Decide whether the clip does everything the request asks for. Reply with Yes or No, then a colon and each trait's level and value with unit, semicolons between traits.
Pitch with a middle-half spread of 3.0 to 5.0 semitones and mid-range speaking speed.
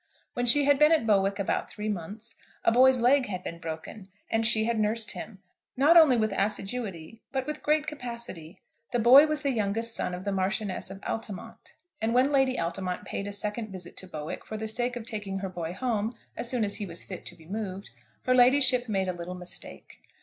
No: average, 4.4 semitones; fast, 215 wpm